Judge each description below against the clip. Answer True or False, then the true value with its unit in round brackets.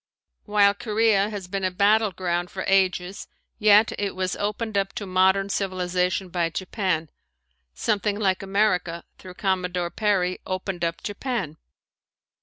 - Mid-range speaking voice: False (195 Hz)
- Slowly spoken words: True (130 wpm)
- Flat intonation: True (2.2 semitones)